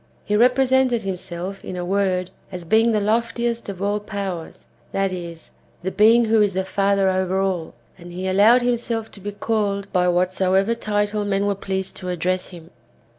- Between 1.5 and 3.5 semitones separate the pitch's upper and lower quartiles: Yes, average, 2.8 semitones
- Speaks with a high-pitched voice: Yes, high, 195 Hz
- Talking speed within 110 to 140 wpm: No, average, 175 wpm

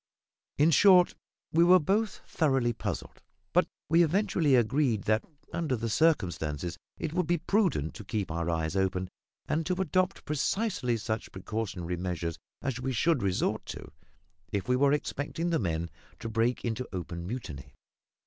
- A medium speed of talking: Yes, average, 155 wpm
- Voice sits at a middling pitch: No, low, 120 Hz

